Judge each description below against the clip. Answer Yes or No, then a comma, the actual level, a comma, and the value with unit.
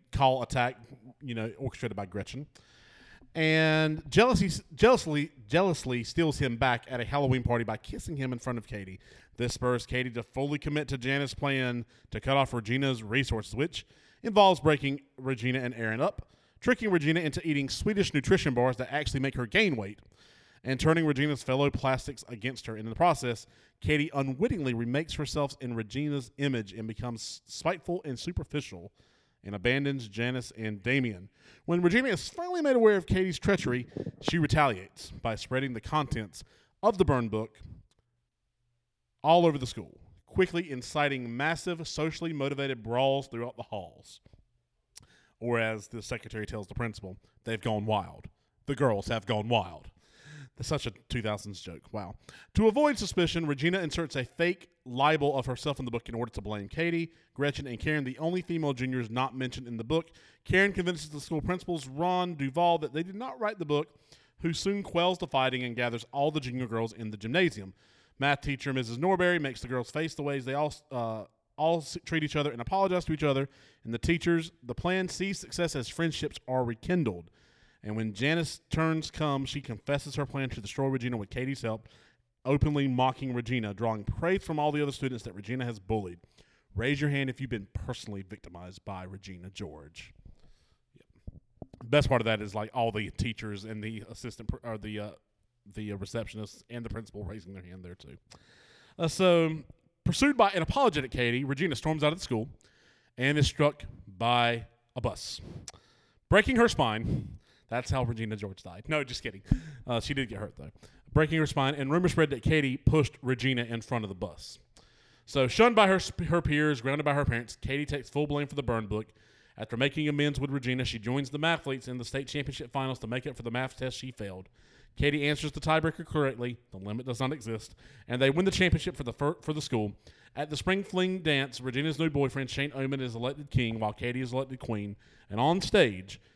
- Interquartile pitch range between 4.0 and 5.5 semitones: Yes, average, 4.8 semitones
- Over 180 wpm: Yes, average, 190 wpm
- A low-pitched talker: Yes, low, 130 Hz